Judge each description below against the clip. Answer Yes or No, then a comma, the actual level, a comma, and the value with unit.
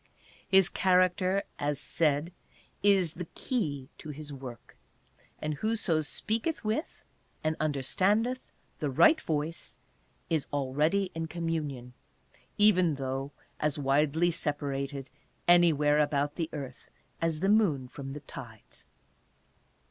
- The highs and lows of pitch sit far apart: No, average, 4.5 semitones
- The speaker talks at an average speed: No, slow, 120 wpm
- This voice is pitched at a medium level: Yes, medium, 155 Hz